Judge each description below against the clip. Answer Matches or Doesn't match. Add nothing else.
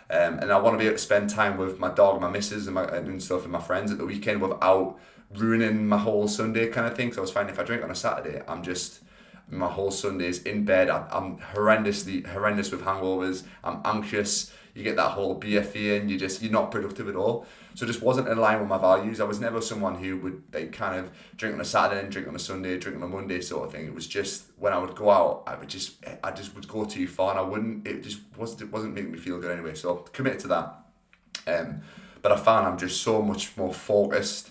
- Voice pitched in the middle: Doesn't match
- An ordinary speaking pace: Doesn't match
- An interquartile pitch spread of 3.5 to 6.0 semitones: Doesn't match